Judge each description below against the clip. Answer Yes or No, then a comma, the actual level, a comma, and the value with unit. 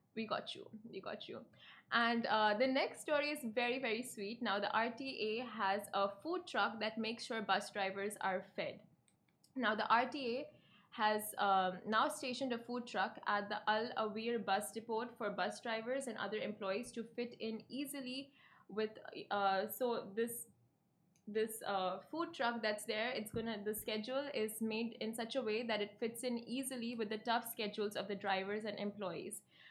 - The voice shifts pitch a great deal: No, average, 2.7 semitones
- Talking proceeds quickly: Yes, fast, 180 wpm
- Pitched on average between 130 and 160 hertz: No, high, 220 Hz